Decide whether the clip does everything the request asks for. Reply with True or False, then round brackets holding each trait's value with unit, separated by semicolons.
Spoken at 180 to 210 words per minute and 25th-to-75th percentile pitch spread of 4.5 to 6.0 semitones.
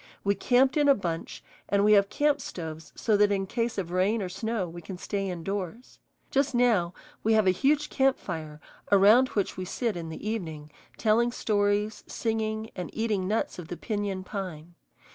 False (185 wpm; 3.9 semitones)